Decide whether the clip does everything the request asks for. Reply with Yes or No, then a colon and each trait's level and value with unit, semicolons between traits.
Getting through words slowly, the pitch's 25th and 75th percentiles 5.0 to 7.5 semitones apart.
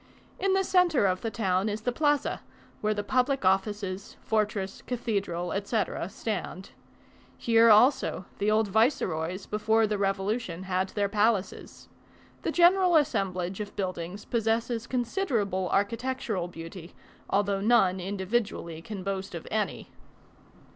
No: slow, 125 wpm; average, 3.5 semitones